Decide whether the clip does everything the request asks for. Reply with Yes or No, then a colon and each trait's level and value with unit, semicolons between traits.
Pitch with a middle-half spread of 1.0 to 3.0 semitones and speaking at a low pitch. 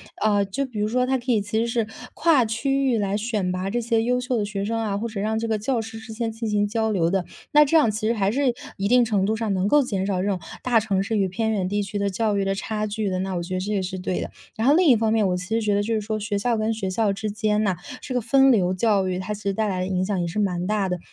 No: average, 2.7 semitones; high, 215 Hz